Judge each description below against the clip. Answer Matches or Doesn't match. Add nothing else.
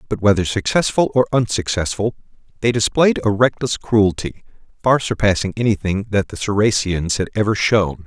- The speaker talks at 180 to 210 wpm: Doesn't match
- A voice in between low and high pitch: Doesn't match